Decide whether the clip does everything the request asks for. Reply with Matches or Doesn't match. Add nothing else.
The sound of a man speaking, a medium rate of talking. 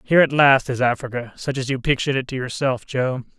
Doesn't match